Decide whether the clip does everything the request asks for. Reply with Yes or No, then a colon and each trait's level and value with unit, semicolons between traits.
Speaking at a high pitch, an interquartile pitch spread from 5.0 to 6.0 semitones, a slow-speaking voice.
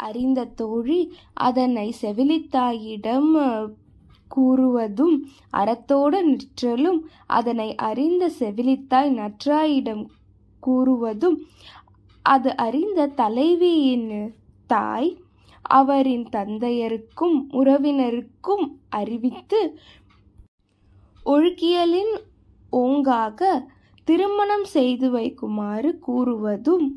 Yes: very high, 260 Hz; average, 5.3 semitones; slow, 60 wpm